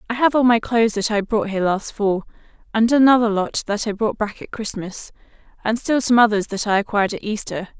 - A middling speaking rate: No, fast, 225 wpm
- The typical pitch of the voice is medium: No, high, 220 Hz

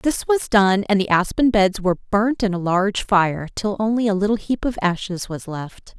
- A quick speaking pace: Yes, fast, 220 wpm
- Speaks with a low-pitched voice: No, high, 200 Hz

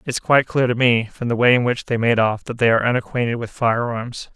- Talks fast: Yes, fast, 275 wpm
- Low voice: Yes, low, 120 Hz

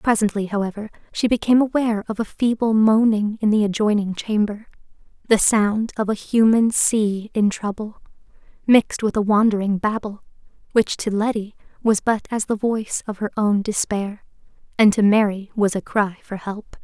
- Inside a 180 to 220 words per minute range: No, average, 160 wpm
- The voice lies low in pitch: No, high, 210 Hz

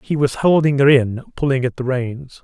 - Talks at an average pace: No, fast, 220 wpm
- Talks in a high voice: No, low, 135 Hz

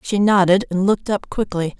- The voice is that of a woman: Yes, female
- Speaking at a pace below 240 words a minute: Yes, average, 200 wpm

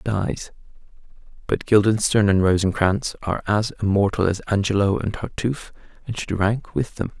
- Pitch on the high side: No, low, 105 Hz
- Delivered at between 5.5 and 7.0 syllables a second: No, 5.0 syllables/s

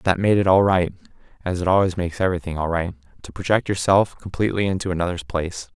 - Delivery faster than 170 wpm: Yes, average, 185 wpm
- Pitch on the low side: Yes, very low, 90 Hz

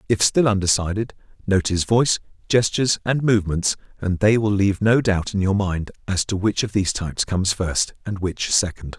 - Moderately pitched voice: No, low, 100 Hz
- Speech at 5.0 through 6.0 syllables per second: Yes, 5.5 syllables/s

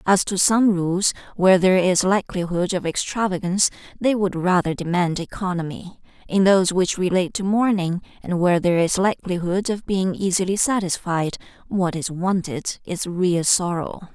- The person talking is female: Yes, female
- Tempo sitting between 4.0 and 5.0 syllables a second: No, 5.2 syllables/s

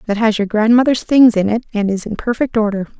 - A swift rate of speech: Yes, fast, 240 wpm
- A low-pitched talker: No, high, 220 Hz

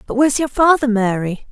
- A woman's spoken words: Yes, female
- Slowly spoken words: No, average, 200 wpm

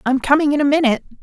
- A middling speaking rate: No, fast, 245 wpm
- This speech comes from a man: No, female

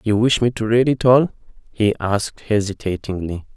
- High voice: No, low, 110 Hz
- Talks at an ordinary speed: Yes, average, 170 wpm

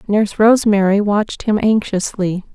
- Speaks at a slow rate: Yes, slow, 120 wpm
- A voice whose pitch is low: No, high, 205 Hz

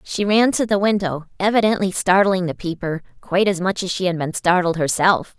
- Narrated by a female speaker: Yes, female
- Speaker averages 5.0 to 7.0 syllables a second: Yes, 5.4 syllables/s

